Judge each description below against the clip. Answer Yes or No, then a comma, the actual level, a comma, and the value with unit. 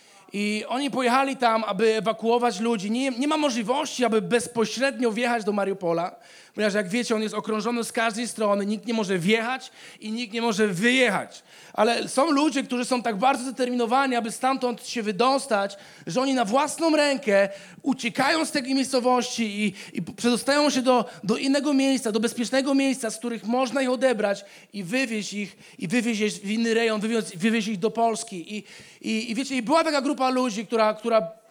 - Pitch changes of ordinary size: Yes, average, 3.1 semitones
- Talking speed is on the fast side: Yes, fast, 185 wpm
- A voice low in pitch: No, high, 235 Hz